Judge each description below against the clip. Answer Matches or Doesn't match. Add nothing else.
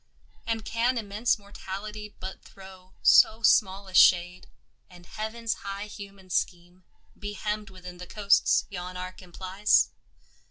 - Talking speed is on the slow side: Matches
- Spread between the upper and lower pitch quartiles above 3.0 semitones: Doesn't match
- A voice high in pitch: Matches